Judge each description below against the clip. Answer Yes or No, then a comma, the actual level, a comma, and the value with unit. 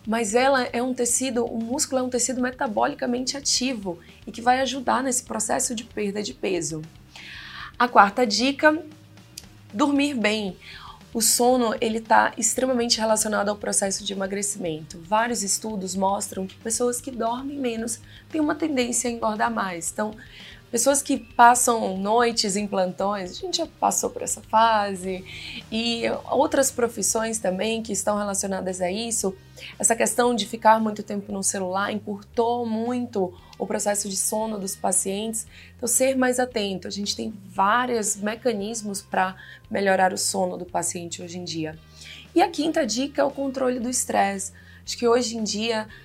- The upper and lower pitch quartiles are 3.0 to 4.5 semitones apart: Yes, average, 4.0 semitones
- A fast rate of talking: No, average, 160 wpm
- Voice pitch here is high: Yes, high, 225 Hz